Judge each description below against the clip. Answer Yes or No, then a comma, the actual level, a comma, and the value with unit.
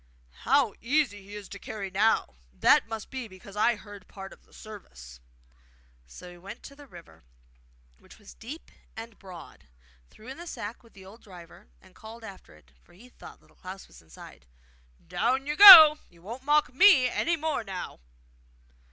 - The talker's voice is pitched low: No, high, 215 Hz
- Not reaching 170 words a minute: No, average, 180 wpm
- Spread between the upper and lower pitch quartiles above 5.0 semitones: Yes, wide, 5.6 semitones